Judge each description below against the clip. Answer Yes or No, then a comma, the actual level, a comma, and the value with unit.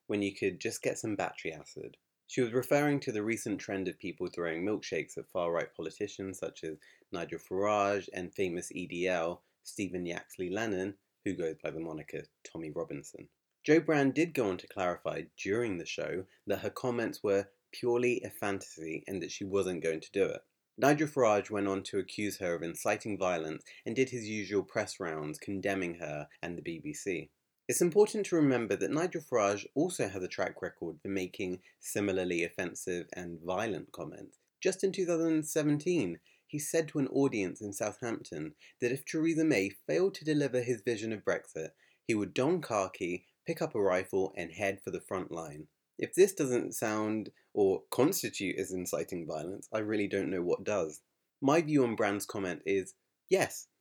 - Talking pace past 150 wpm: Yes, average, 180 wpm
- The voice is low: Yes, low, 105 Hz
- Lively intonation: Yes, wide, 6.9 semitones